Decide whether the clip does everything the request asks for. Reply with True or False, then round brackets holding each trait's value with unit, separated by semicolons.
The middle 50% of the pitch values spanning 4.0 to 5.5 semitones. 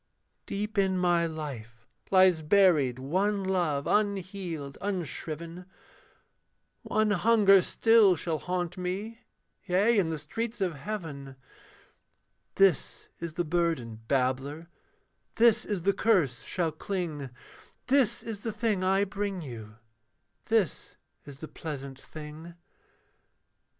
True (5.0 semitones)